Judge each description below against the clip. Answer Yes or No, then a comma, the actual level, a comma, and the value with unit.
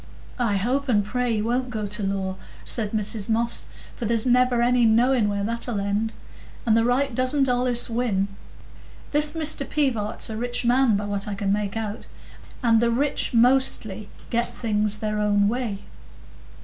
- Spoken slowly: No, average, 170 wpm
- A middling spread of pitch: Yes, average, 3.1 semitones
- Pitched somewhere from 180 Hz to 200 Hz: No, high, 230 Hz